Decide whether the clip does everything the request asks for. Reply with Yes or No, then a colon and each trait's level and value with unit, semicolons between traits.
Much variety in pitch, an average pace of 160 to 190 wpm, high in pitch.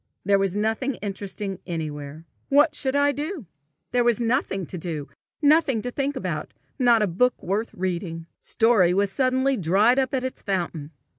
Yes: wide, 6.1 semitones; average, 165 wpm; high, 215 Hz